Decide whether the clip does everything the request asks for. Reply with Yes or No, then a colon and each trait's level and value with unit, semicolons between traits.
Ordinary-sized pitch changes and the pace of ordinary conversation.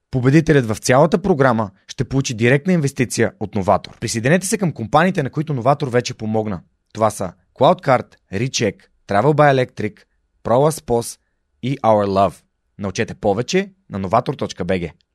No: wide, 5.8 semitones; average, 135 wpm